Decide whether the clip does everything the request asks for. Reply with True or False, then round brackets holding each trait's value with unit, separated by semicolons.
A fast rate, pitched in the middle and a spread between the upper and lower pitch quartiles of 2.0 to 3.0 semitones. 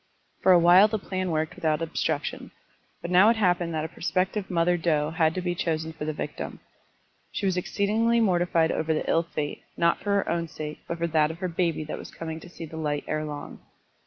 True (225 wpm; 170 Hz; 2.6 semitones)